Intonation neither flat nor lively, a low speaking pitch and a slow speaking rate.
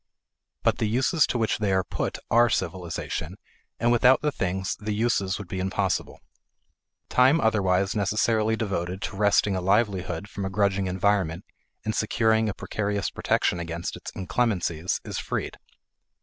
No: average, 3.0 semitones; low, 100 Hz; average, 150 wpm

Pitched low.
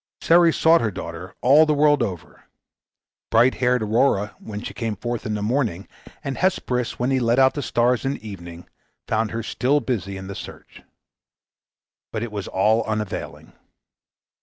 Yes: low, 115 Hz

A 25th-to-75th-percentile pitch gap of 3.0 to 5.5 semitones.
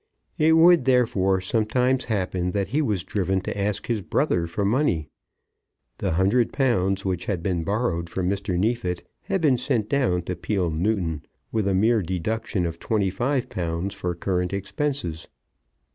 Yes: average, 4.8 semitones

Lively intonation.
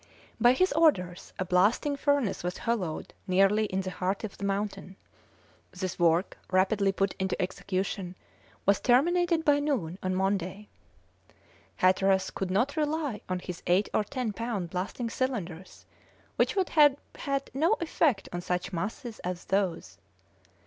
Yes: wide, 5.9 semitones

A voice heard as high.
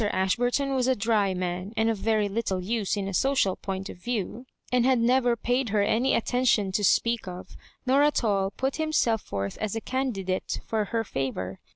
Yes: high, 220 Hz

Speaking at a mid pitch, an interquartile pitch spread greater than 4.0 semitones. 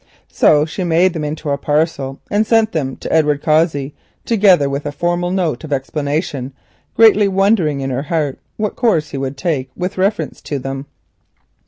Yes: medium, 155 Hz; average, 4.6 semitones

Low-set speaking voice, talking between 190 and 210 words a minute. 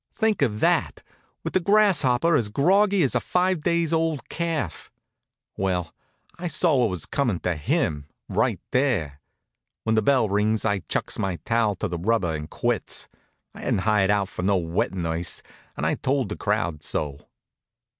No: low, 110 Hz; average, 170 wpm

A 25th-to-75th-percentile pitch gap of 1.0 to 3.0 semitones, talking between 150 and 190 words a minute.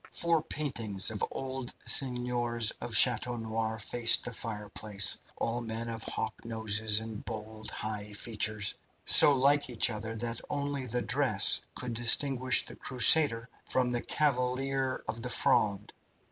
No: narrow, 2.6 semitones; average, 140 wpm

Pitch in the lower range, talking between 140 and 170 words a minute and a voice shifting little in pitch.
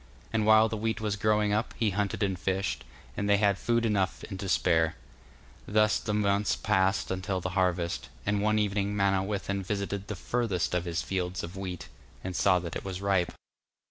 No: low, 100 Hz; average, 190 wpm; narrow, 2.2 semitones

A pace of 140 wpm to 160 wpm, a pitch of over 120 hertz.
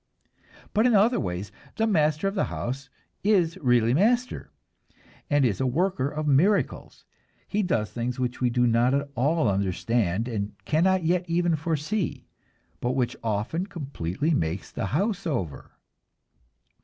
Yes: average, 145 wpm; medium, 140 Hz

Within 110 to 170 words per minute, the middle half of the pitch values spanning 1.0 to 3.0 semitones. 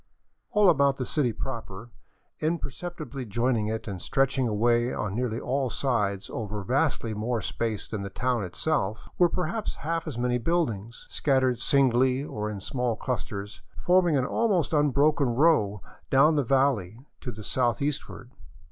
No: average, 155 wpm; average, 4.6 semitones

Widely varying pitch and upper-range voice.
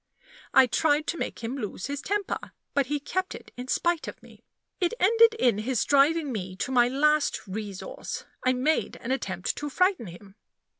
Yes: wide, 5.8 semitones; very high, 275 Hz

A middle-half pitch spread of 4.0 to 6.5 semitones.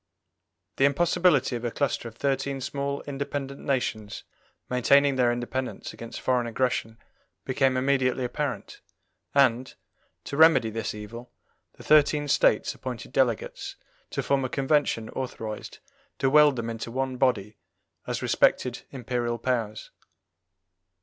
No: average, 2.9 semitones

